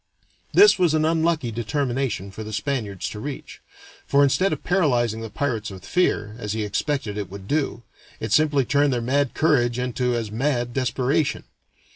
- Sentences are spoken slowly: No, average, 170 wpm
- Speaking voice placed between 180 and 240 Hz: No, low, 125 Hz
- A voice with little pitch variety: No, average, 4.8 semitones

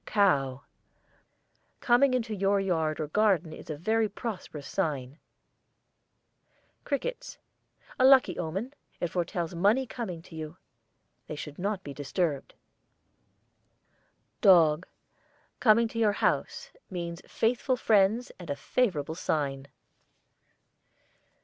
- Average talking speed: No, slow, 105 wpm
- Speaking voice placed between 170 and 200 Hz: Yes, medium, 185 Hz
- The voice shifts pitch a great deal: Yes, wide, 6.1 semitones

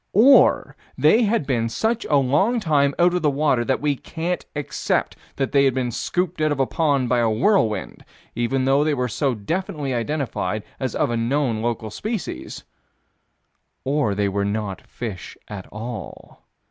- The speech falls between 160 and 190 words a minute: Yes, average, 170 wpm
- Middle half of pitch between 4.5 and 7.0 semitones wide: Yes, average, 5.0 semitones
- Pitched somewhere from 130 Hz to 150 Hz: Yes, low, 135 Hz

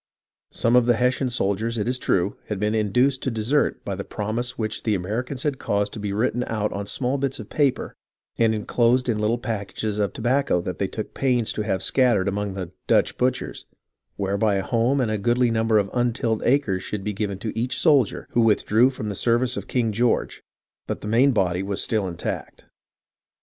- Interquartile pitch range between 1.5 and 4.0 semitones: Yes, average, 3.3 semitones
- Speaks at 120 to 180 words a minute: No, fast, 205 wpm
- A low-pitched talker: Yes, low, 110 Hz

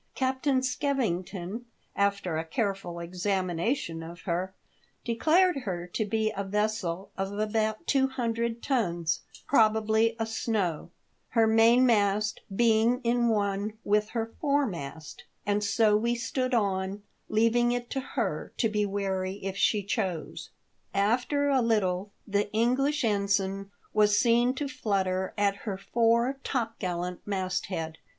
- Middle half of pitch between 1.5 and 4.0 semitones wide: Yes, average, 3.6 semitones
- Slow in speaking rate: Yes, slow, 130 wpm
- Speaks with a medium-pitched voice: No, high, 210 Hz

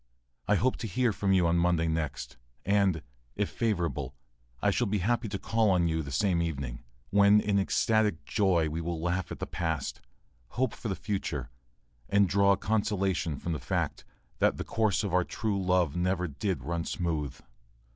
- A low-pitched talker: Yes, very low, 95 Hz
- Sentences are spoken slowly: No, average, 175 wpm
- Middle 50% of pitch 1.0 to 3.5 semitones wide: No, average, 3.9 semitones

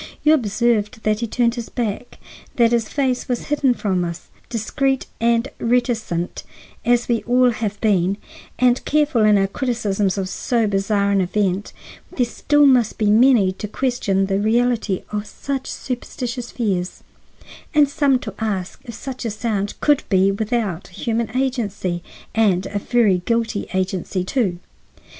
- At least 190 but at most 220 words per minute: No, average, 150 wpm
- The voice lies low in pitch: No, high, 225 Hz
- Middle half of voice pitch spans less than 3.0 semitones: No, average, 3.8 semitones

